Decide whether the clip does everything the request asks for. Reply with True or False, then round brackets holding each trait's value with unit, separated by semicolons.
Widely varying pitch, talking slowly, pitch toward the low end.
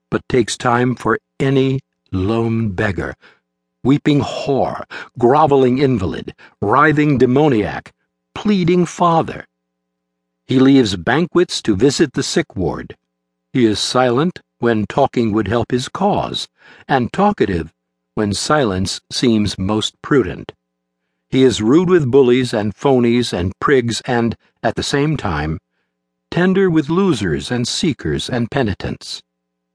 True (7.7 semitones; 120 wpm; 120 Hz)